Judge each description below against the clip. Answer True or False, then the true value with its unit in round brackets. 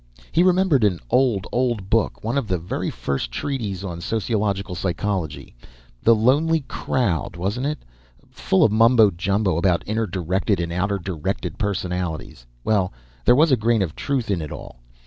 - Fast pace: False (165 wpm)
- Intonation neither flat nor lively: True (4.7 semitones)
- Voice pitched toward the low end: True (100 Hz)